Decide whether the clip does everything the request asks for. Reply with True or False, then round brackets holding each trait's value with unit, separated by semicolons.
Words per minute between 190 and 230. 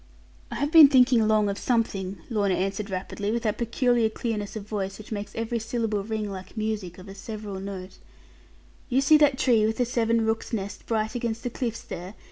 True (200 wpm)